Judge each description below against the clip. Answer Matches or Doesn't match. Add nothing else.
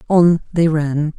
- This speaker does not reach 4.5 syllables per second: Matches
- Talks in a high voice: Doesn't match